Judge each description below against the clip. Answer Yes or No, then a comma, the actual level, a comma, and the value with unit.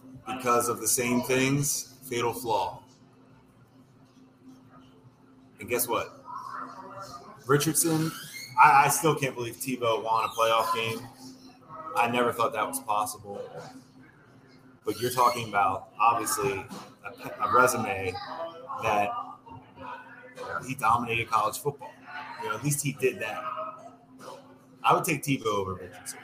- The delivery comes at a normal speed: No, slow, 125 wpm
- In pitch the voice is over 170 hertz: No, low, 130 Hz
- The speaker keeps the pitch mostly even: Yes, narrow, 2.3 semitones